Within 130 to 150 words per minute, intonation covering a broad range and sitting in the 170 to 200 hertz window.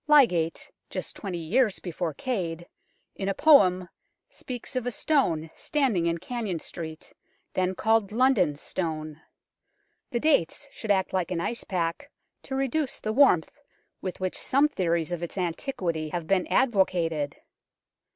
Yes: average, 140 wpm; wide, 6.8 semitones; medium, 185 Hz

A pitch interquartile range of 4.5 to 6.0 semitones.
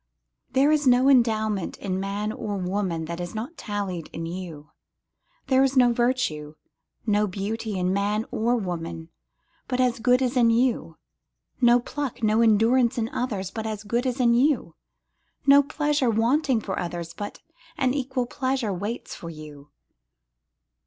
Yes: average, 4.9 semitones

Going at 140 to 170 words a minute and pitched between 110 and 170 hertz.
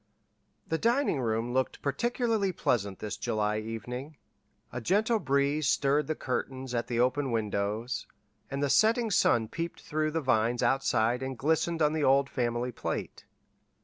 Yes: average, 150 wpm; low, 135 Hz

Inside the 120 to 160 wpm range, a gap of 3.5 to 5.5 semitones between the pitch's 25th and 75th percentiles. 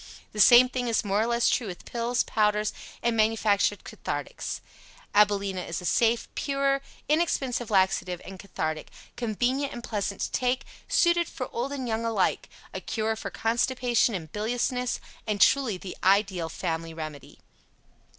Yes: average, 155 wpm; average, 4.1 semitones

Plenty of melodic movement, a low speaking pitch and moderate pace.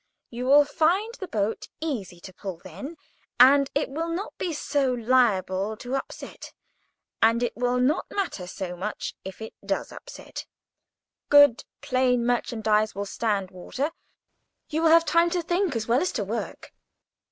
No: wide, 6.1 semitones; very high, 250 Hz; average, 160 wpm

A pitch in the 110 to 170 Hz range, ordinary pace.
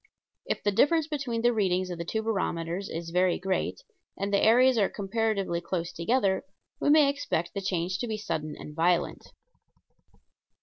No: high, 195 Hz; average, 170 wpm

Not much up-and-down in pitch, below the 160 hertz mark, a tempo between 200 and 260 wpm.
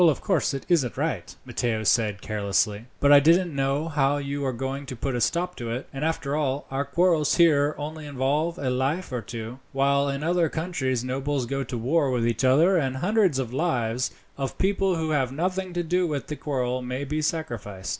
No: average, 3.9 semitones; medium, 140 Hz; fast, 205 wpm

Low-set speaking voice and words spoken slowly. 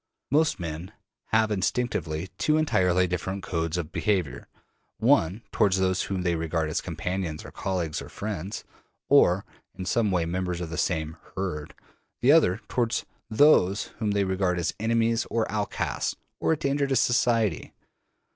No: very low, 95 Hz; average, 155 wpm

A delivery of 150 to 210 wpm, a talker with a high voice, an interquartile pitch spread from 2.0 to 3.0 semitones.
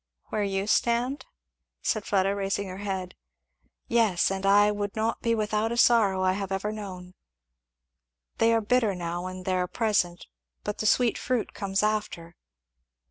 Yes: average, 160 wpm; high, 205 Hz; narrow, 2.6 semitones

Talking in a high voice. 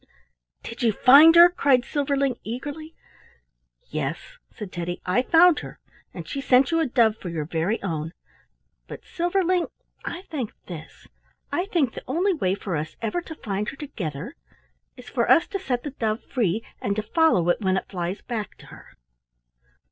Yes: high, 245 Hz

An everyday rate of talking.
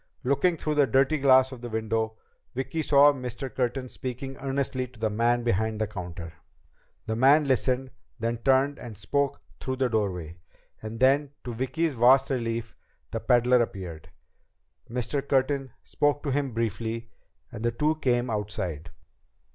Yes: average, 155 wpm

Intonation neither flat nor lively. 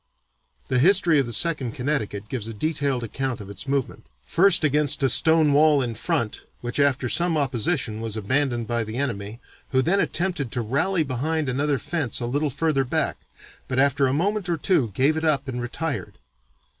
Yes: average, 4.5 semitones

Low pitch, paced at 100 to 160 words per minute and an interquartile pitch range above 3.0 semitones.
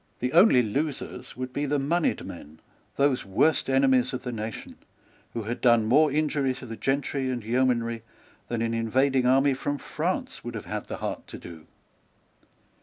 No: low, 130 Hz; average, 175 wpm; average, 3.4 semitones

